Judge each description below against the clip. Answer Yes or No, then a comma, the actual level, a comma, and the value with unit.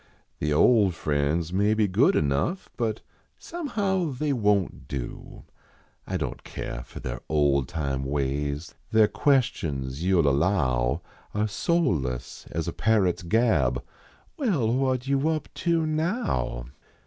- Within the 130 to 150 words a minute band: Yes, average, 145 wpm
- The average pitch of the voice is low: Yes, very low, 95 Hz